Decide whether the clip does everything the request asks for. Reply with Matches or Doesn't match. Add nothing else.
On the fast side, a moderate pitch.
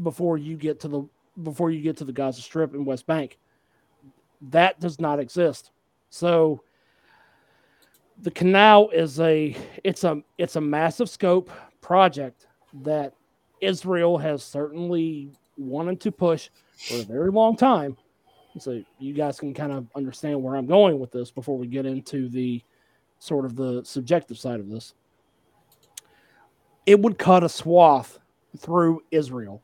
Doesn't match